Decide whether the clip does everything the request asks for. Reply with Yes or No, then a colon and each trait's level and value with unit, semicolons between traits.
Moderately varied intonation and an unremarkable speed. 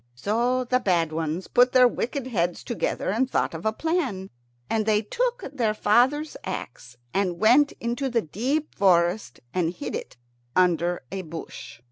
No: wide, 6.4 semitones; average, 160 wpm